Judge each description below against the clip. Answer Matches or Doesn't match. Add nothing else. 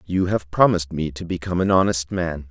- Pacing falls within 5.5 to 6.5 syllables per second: Matches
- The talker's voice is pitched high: Doesn't match